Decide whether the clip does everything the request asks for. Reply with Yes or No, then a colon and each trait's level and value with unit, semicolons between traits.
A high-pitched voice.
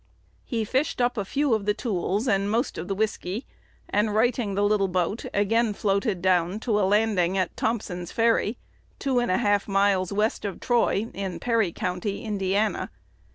Yes: high, 205 Hz